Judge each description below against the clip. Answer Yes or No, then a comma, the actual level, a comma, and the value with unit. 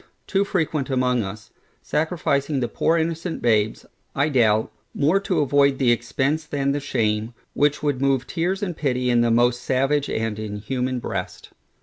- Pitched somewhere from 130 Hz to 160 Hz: Yes, low, 135 Hz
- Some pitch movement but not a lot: Yes, average, 4.1 semitones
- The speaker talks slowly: No, average, 160 wpm